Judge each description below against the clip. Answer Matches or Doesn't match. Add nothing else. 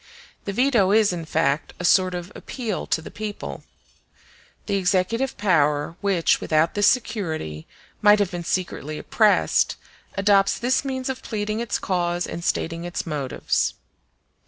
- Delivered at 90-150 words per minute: Matches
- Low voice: Doesn't match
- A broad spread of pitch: Doesn't match